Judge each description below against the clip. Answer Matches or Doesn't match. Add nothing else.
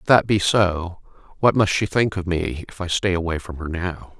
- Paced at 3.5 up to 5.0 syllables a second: Matches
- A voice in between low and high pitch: Doesn't match